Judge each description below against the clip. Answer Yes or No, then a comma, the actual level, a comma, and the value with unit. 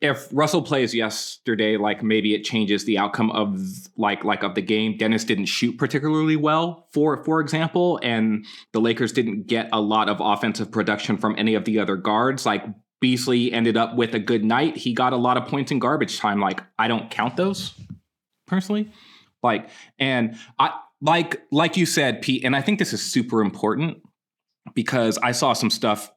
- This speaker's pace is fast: No, average, 190 wpm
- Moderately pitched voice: No, low, 120 Hz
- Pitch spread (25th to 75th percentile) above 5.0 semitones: Yes, wide, 5.5 semitones